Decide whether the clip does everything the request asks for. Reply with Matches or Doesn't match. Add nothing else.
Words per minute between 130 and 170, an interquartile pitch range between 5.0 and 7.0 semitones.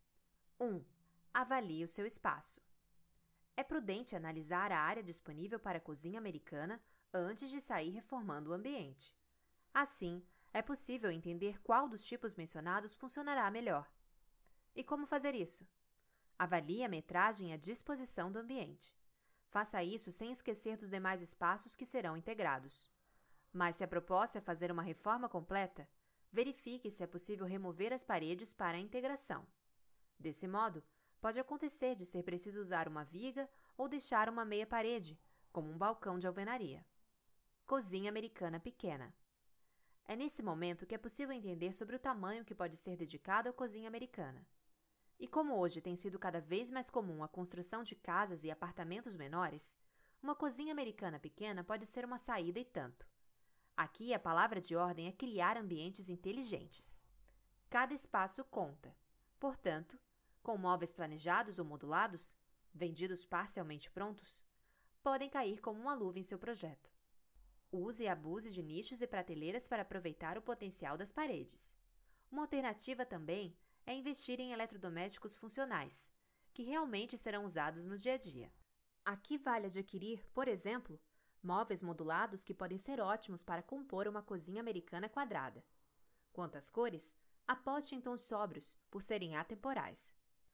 Matches